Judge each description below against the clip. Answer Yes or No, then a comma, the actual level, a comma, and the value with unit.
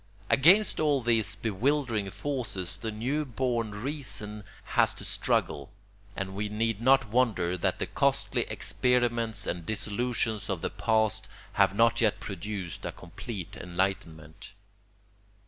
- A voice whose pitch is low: Yes, low, 110 Hz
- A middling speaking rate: No, slow, 130 wpm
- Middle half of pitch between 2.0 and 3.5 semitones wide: No, average, 4.0 semitones